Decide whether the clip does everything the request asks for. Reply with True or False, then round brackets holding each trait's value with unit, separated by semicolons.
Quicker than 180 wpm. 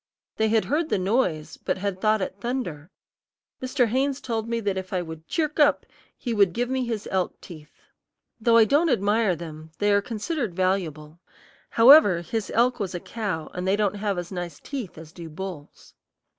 True (190 wpm)